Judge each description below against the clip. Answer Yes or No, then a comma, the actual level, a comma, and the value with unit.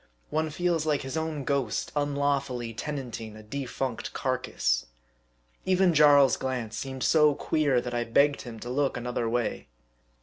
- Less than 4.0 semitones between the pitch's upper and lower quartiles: Yes, average, 3.4 semitones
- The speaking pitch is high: No, low, 135 Hz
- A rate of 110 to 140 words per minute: No, average, 155 wpm